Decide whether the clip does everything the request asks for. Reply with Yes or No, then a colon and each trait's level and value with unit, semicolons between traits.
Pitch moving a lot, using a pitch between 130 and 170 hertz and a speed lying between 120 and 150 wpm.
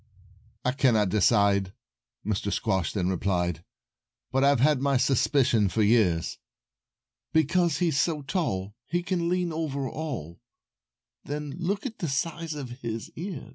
Yes: wide, 7.9 semitones; low, 135 Hz; slow, 135 wpm